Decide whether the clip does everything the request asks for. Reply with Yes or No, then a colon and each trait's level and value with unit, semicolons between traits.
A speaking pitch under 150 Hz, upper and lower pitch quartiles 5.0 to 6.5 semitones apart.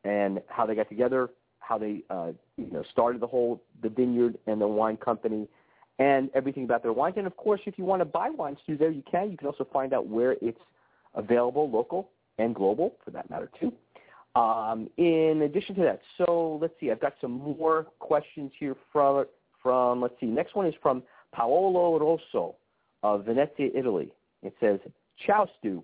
Yes: low, 135 Hz; wide, 5.5 semitones